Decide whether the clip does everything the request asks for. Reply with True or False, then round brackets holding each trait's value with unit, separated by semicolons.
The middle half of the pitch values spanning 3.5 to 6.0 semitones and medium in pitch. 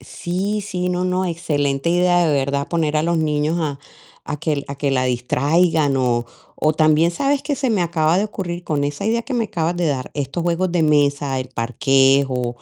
True (4.0 semitones; 155 Hz)